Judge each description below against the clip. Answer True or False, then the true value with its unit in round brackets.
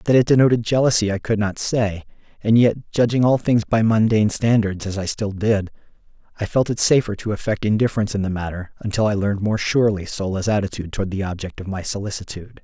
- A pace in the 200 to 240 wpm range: True (205 wpm)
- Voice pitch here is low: True (105 Hz)